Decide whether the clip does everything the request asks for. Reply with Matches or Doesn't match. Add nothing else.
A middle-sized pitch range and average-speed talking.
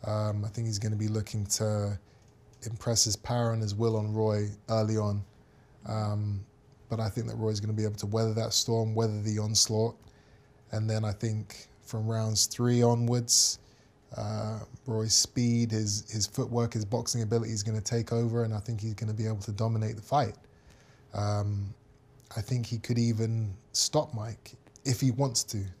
Doesn't match